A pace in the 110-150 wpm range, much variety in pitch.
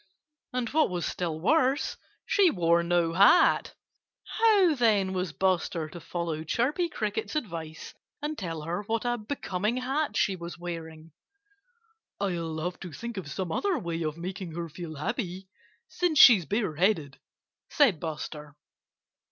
Yes: average, 145 wpm; wide, 6.4 semitones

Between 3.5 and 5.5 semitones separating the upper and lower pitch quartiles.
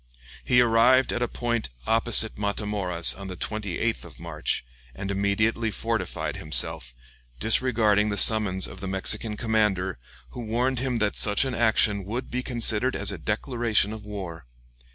No: average, 2.9 semitones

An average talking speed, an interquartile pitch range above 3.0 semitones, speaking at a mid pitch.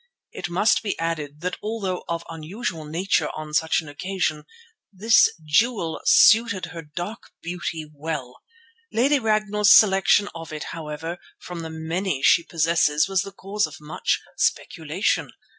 Yes: average, 145 wpm; average, 4.2 semitones; medium, 170 Hz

